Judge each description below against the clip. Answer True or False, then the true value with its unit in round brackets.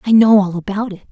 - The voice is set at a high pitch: True (200 Hz)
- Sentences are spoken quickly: True (270 wpm)